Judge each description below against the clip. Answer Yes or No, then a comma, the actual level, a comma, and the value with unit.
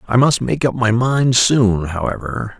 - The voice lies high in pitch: No, low, 115 Hz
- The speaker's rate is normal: Yes, average, 185 wpm